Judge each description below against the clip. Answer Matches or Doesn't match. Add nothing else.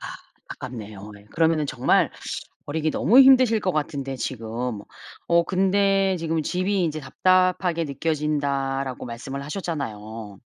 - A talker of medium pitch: Matches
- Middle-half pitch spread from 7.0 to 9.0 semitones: Doesn't match